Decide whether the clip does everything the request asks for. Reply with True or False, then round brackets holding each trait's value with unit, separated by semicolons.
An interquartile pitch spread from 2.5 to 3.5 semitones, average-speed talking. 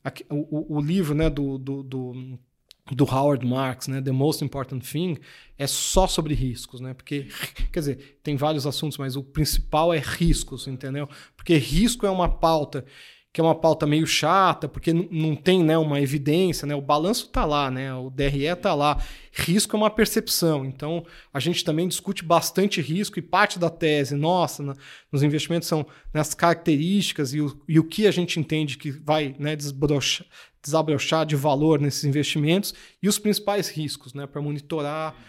True (3.2 semitones; 180 wpm)